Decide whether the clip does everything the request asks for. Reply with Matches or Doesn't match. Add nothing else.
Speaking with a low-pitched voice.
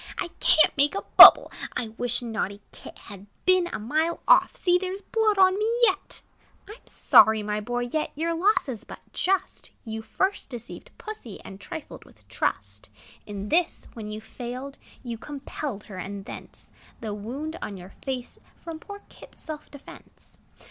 Doesn't match